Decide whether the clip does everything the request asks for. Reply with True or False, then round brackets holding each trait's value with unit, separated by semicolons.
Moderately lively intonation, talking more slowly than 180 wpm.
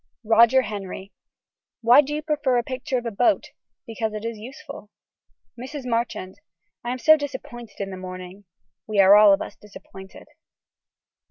True (4.3 semitones; 160 wpm)